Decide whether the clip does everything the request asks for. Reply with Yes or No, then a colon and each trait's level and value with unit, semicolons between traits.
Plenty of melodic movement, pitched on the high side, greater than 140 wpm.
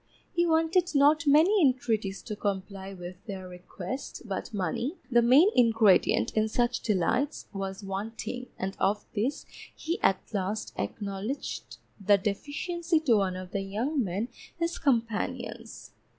No: wide, 6.3 semitones; high, 220 Hz; slow, 135 wpm